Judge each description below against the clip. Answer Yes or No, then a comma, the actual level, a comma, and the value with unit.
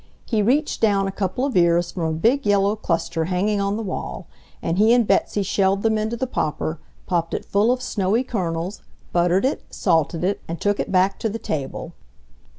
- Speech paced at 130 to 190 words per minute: No, average, 200 wpm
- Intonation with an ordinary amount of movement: Yes, average, 4.0 semitones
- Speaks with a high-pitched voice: Yes, high, 195 Hz